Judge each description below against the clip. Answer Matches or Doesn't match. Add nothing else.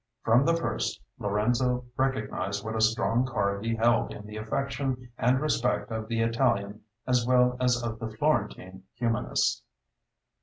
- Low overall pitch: Matches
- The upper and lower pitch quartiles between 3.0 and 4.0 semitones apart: Doesn't match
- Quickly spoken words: Doesn't match